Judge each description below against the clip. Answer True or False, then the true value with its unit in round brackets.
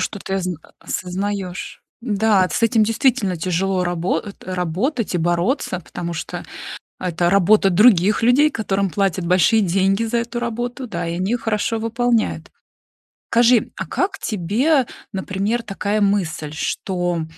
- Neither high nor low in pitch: False (200 Hz)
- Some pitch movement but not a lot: True (4.2 semitones)